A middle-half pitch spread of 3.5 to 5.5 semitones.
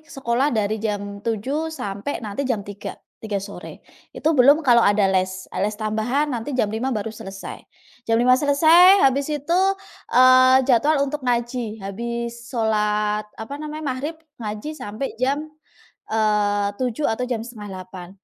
Yes: average, 3.9 semitones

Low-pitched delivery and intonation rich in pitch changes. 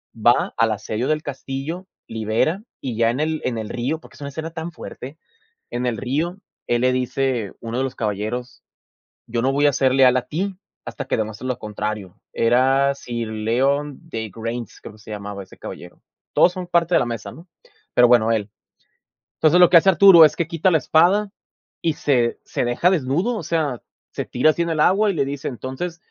Yes: low, 130 Hz; wide, 5.7 semitones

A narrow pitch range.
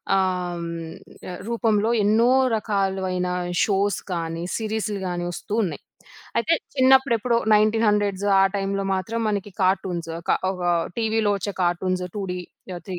No: average, 3.0 semitones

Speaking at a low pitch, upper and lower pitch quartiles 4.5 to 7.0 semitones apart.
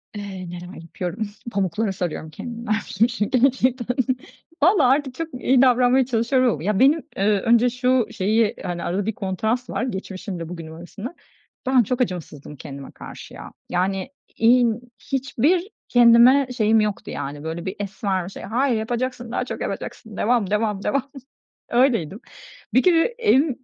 No: high, 225 Hz; average, 4.9 semitones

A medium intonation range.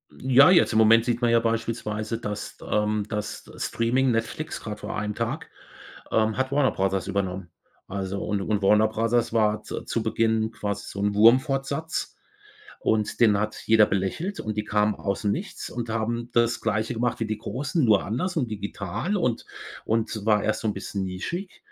No: narrow, 2.3 semitones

